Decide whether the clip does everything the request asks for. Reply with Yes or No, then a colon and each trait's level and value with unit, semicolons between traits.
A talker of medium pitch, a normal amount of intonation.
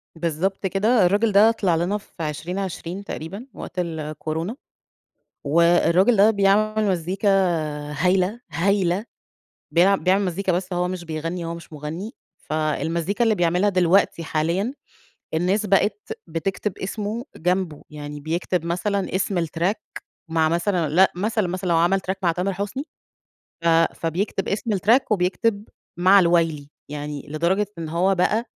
Yes: medium, 180 Hz; average, 3.3 semitones